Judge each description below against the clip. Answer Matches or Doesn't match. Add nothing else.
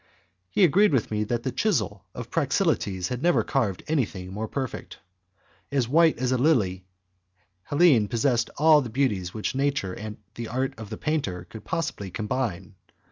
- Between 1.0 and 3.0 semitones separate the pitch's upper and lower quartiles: Doesn't match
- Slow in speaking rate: Doesn't match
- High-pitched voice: Doesn't match